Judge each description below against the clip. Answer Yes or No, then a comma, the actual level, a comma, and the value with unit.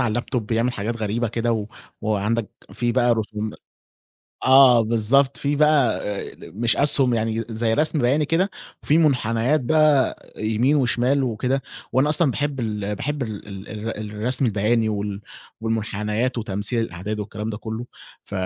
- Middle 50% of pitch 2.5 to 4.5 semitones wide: Yes, average, 3.7 semitones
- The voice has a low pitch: Yes, low, 115 Hz